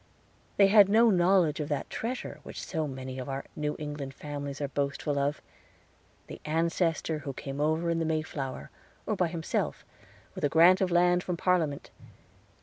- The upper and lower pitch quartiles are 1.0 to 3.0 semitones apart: No, average, 3.8 semitones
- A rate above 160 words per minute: Yes, average, 170 wpm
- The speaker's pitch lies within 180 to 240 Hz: No, medium, 155 Hz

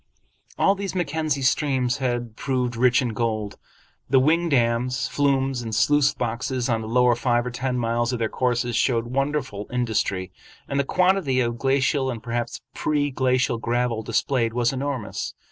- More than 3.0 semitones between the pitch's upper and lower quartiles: No, narrow, 2.6 semitones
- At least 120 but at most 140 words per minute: No, average, 160 wpm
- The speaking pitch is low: Yes, low, 125 Hz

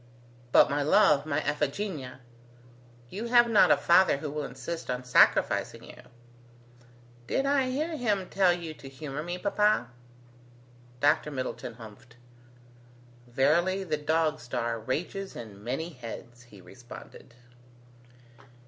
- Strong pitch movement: Yes, wide, 6.9 semitones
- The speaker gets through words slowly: Yes, slow, 125 wpm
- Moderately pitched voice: Yes, medium, 150 Hz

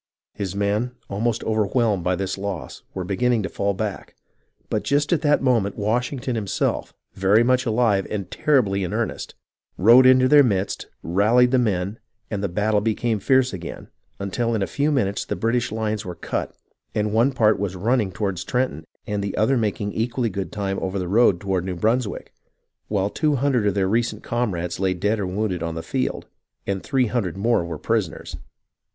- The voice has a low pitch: Yes, low, 105 Hz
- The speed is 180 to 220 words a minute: Yes, average, 185 wpm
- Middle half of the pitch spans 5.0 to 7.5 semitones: No, average, 3.7 semitones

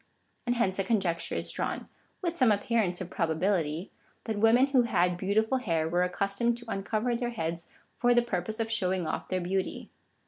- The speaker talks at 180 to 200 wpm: Yes, average, 195 wpm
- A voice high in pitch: Yes, high, 200 Hz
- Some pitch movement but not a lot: Yes, average, 4.8 semitones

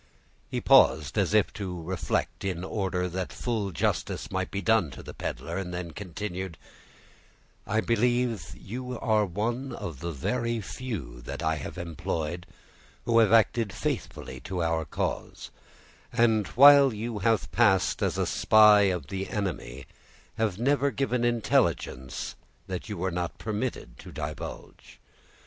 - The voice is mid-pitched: No, low, 100 Hz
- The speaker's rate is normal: Yes, average, 145 wpm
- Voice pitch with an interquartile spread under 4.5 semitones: No, average, 5.2 semitones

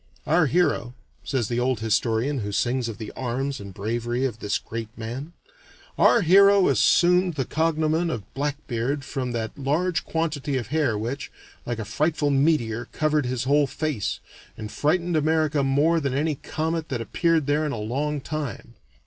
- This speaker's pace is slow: No, average, 165 wpm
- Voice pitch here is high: No, medium, 140 Hz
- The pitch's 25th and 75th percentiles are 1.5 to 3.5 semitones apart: No, average, 4.8 semitones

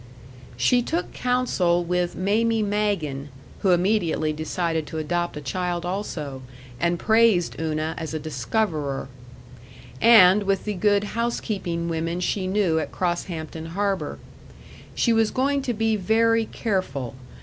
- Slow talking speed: Yes, slow, 130 wpm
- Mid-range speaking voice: Yes, medium, 180 Hz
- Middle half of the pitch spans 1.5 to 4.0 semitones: No, average, 4.9 semitones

